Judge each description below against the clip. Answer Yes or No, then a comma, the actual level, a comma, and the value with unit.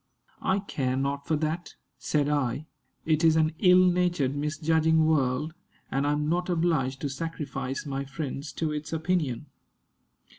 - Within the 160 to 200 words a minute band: No, average, 150 wpm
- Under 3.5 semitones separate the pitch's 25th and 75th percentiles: Yes, average, 2.8 semitones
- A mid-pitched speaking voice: Yes, medium, 150 Hz